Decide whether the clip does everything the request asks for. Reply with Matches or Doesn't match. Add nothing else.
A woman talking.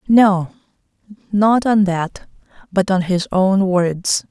Matches